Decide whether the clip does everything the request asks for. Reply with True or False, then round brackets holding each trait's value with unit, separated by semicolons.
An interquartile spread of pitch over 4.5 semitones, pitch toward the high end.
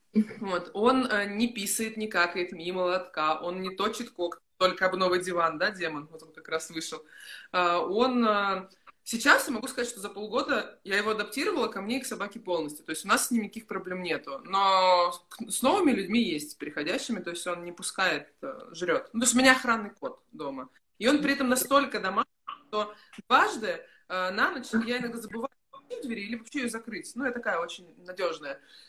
True (5.3 semitones; 205 Hz)